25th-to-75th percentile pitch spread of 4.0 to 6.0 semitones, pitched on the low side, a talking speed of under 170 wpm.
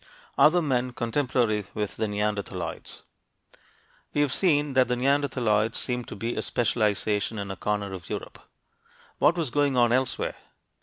Yes: average, 4.5 semitones; low, 120 Hz; average, 150 wpm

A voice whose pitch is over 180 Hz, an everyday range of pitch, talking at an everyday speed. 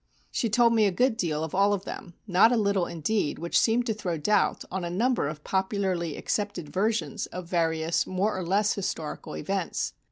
Yes: high, 190 Hz; average, 3.8 semitones; average, 195 wpm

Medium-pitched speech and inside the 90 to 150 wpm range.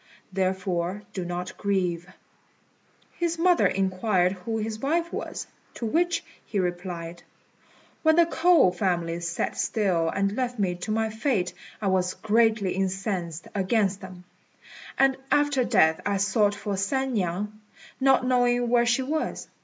No: high, 200 Hz; average, 140 wpm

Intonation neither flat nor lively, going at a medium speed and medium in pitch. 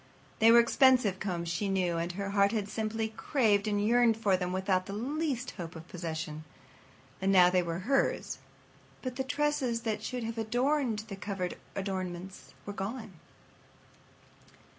No: average, 4.1 semitones; average, 160 wpm; high, 205 Hz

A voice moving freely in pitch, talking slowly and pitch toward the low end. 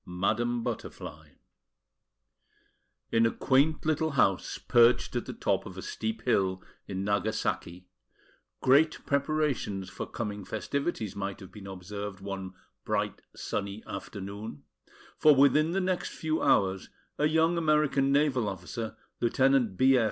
Yes: wide, 6.3 semitones; slow, 130 wpm; low, 115 Hz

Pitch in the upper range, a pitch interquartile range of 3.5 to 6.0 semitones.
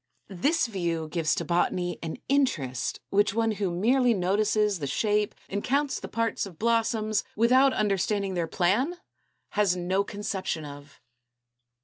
Yes: high, 205 Hz; average, 4.5 semitones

